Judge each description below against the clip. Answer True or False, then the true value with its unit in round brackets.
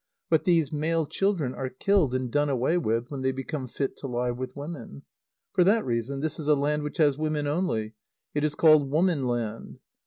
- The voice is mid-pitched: True (145 Hz)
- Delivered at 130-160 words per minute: False (205 wpm)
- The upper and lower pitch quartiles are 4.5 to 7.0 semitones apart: False (3.4 semitones)